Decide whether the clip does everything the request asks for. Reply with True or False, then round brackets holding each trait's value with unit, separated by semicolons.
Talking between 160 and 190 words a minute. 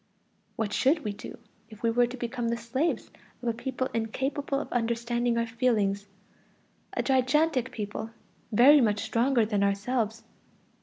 False (150 wpm)